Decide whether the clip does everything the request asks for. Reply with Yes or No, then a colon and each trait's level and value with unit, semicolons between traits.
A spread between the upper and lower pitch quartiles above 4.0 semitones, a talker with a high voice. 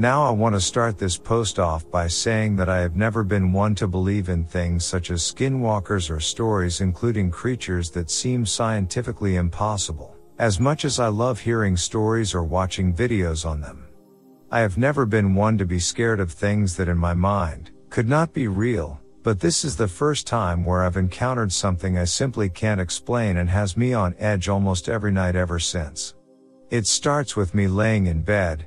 No: average, 4.5 semitones; low, 100 Hz